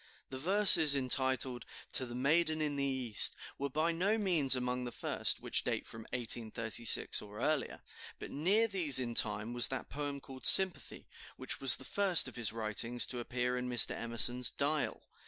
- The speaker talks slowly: No, average, 175 wpm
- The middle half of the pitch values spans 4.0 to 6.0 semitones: Yes, average, 4.3 semitones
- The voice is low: Yes, low, 130 Hz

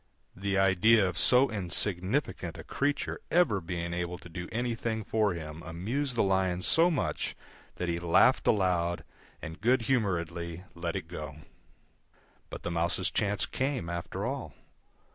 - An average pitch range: Yes, average, 4.6 semitones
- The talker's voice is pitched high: No, very low, 95 Hz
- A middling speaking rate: Yes, average, 145 wpm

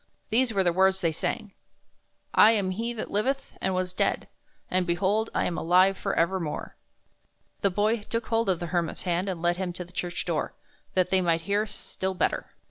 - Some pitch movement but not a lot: Yes, average, 3.0 semitones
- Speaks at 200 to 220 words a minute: Yes, fast, 205 wpm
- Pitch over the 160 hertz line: Yes, high, 190 Hz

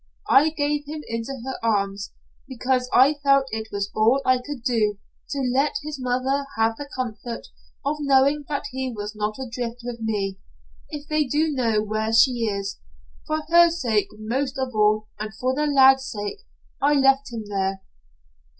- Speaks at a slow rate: No, average, 170 wpm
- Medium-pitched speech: No, very high, 255 Hz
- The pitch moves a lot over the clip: No, average, 4.3 semitones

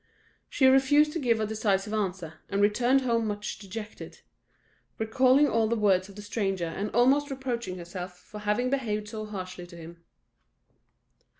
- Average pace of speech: Yes, average, 160 wpm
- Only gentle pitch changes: No, average, 4.2 semitones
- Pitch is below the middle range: No, high, 215 Hz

